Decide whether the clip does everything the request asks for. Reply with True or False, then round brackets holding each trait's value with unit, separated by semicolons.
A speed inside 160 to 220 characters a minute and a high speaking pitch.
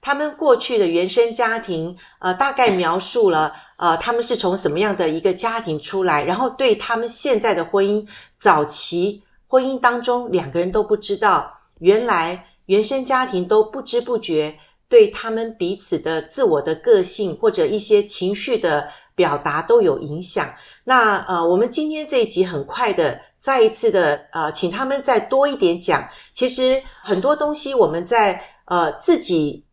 False (250 characters per minute; 230 Hz)